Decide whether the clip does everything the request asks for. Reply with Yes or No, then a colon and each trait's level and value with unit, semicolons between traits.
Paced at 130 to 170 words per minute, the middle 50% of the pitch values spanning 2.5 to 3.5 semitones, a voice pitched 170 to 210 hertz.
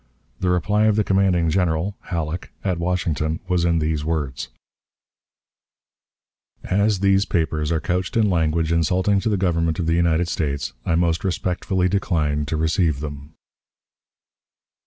No: average, 140 wpm; average, 2.9 semitones; very low, 85 Hz